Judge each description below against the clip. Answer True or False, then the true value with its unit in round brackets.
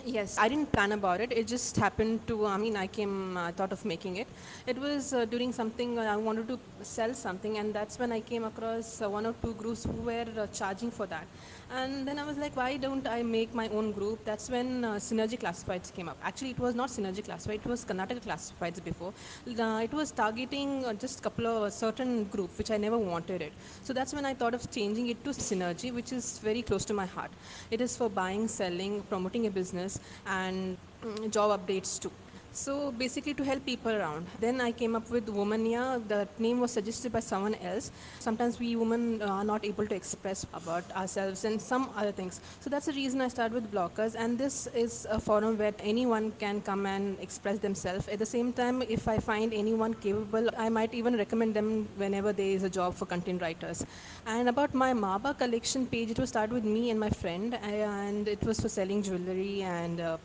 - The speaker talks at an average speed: False (220 wpm)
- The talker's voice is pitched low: False (220 Hz)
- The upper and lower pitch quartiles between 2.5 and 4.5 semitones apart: True (3.0 semitones)